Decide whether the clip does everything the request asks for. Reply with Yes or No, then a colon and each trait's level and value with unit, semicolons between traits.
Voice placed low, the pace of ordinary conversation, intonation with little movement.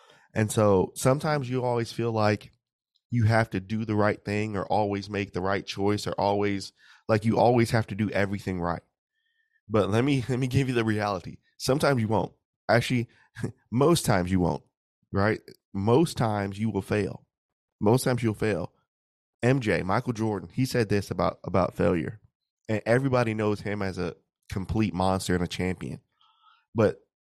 No: low, 110 Hz; average, 170 wpm; average, 3.8 semitones